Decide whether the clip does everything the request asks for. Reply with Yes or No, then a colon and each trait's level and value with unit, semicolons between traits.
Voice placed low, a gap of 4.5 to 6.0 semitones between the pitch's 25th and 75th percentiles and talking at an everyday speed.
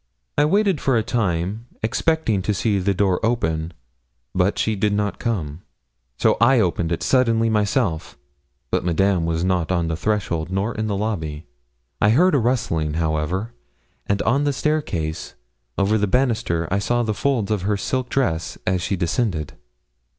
Yes: low, 100 Hz; wide, 5.4 semitones; average, 165 wpm